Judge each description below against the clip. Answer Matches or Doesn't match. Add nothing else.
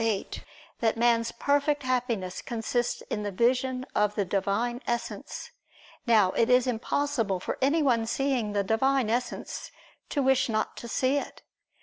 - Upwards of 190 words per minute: Doesn't match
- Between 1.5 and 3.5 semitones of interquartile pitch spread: Matches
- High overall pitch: Matches